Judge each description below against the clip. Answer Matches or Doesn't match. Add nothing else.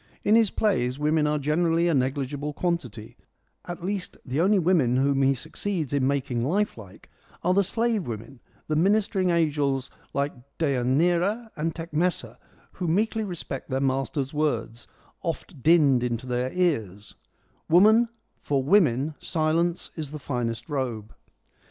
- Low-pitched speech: Doesn't match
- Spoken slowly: Doesn't match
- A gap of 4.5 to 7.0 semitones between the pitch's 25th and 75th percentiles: Matches